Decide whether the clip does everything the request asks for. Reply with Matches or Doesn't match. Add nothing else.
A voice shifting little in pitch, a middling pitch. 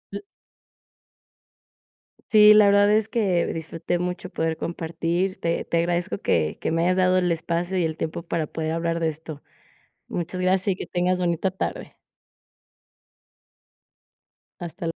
Matches